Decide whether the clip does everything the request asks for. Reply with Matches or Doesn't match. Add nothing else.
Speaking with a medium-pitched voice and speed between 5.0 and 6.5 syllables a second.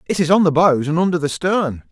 Matches